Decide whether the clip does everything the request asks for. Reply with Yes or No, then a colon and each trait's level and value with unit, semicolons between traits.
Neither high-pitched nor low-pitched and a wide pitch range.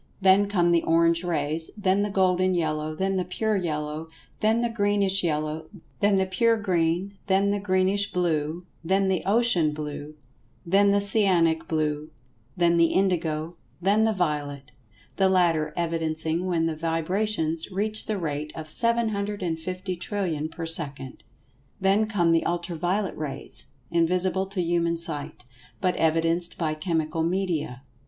No: medium, 175 Hz; average, 3.5 semitones